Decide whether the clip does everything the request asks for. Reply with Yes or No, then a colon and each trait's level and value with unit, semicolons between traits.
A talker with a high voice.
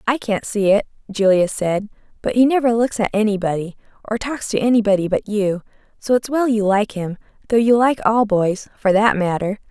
Yes: high, 210 Hz